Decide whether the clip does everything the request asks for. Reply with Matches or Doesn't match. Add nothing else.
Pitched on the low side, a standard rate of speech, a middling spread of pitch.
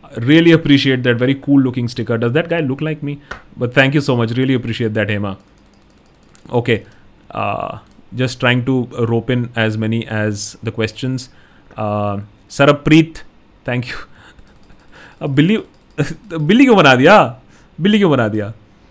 Matches